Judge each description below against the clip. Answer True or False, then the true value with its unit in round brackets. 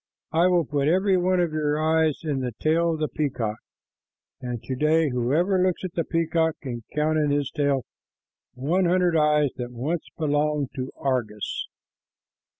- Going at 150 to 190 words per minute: True (165 wpm)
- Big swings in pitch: False (3.5 semitones)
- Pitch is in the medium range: True (150 Hz)